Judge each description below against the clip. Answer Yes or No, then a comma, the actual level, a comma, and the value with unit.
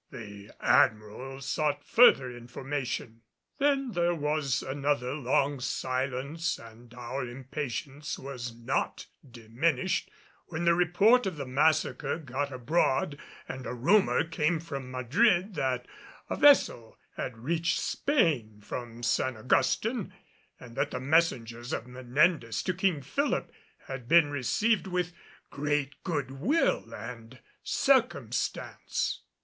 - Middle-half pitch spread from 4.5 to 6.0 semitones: Yes, average, 5.2 semitones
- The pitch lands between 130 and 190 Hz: Yes, low, 135 Hz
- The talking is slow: Yes, slow, 120 wpm